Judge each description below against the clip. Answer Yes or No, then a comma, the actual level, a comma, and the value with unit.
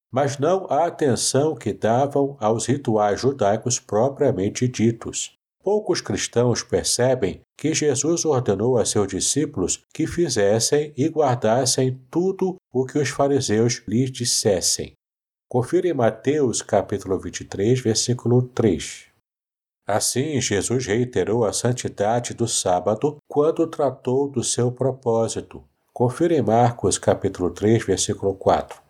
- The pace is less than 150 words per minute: Yes, slow, 120 wpm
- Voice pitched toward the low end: Yes, low, 125 Hz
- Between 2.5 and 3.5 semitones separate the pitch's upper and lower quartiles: No, average, 4.4 semitones